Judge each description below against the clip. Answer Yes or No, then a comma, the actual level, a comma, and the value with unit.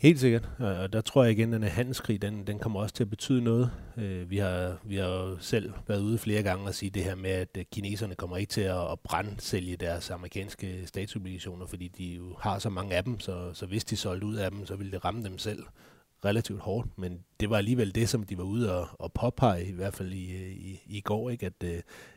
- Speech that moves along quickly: Yes, fast, 240 wpm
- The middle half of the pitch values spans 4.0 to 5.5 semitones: No, average, 3.1 semitones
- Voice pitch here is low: Yes, low, 100 Hz